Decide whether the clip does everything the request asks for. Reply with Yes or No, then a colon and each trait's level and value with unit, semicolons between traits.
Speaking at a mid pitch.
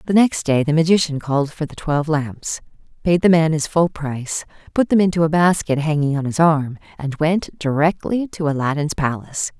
Yes: medium, 155 Hz